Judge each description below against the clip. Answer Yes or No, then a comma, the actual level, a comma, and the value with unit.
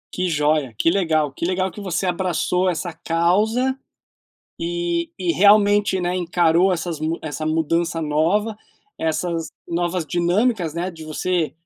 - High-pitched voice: No, medium, 175 Hz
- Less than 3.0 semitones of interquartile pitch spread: Yes, narrow, 2.4 semitones